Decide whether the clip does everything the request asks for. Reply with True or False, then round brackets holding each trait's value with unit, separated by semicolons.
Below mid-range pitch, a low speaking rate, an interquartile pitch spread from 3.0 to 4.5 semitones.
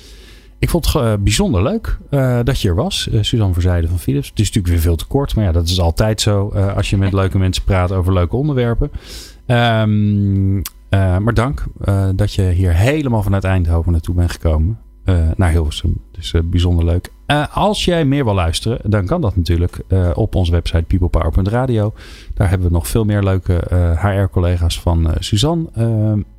False (95 Hz; 200 wpm; 3.9 semitones)